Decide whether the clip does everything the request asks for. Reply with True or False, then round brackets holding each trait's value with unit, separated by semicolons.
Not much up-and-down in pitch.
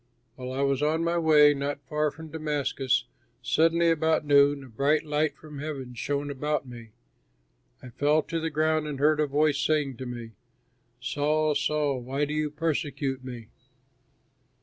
True (2.2 semitones)